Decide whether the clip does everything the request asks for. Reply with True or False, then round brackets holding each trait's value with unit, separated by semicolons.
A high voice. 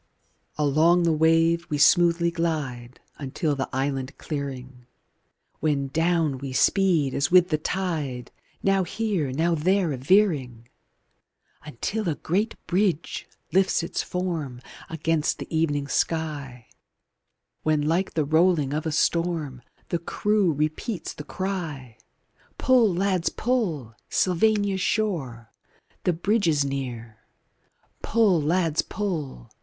False (160 Hz)